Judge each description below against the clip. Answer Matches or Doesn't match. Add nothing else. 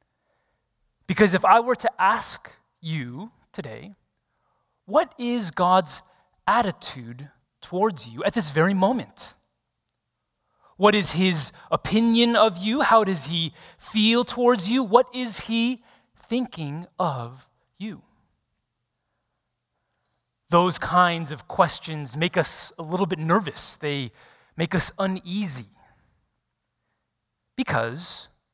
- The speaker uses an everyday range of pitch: Doesn't match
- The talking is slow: Matches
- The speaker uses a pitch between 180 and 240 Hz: Matches